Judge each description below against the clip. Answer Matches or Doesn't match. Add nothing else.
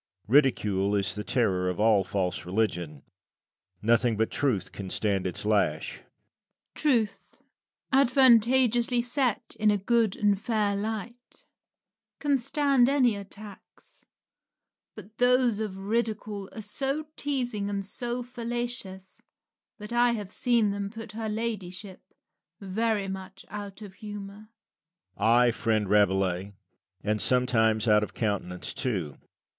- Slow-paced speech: Matches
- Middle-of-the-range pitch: Doesn't match